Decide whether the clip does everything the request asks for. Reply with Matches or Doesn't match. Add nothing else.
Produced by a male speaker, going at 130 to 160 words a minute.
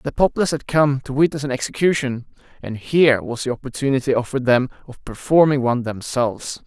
Doesn't match